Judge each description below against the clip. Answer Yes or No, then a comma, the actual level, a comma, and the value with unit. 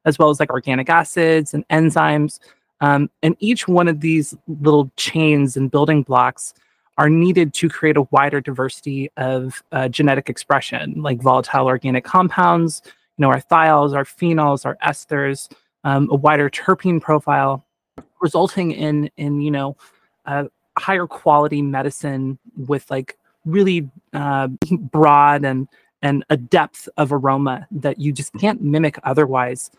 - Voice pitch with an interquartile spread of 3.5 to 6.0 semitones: No, narrow, 2.6 semitones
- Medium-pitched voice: Yes, medium, 145 Hz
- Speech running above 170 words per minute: No, average, 150 wpm